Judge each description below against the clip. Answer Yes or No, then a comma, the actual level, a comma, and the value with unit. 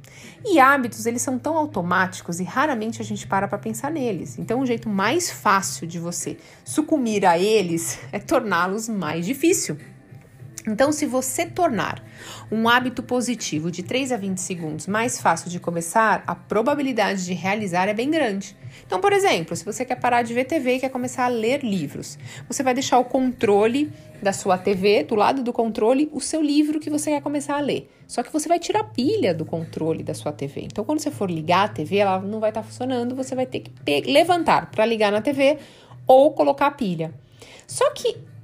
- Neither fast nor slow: No, fast, 200 wpm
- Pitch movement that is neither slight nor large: No, wide, 7.6 semitones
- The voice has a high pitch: Yes, high, 225 Hz